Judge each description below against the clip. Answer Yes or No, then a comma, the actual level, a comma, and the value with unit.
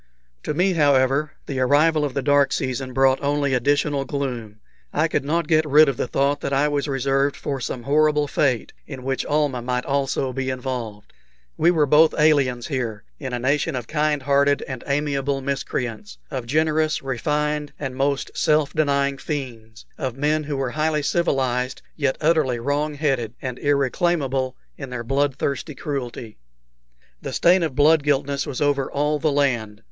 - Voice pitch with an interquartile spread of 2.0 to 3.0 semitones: Yes, narrow, 2.4 semitones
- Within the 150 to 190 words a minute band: Yes, average, 170 wpm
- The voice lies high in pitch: No, medium, 140 Hz